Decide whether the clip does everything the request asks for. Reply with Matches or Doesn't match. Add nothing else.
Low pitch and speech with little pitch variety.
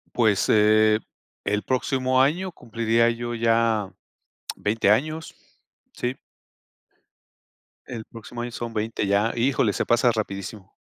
Matches